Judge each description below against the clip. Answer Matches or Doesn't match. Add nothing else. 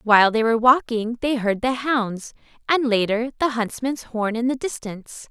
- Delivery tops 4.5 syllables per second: Matches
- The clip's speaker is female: Matches